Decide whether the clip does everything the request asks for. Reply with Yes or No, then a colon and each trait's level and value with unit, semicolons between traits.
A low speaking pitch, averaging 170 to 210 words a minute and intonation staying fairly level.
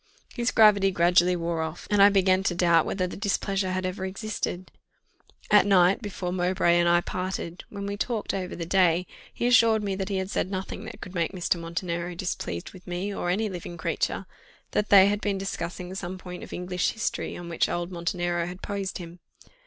No: medium, 185 Hz; average, 200 wpm; narrow, 2.2 semitones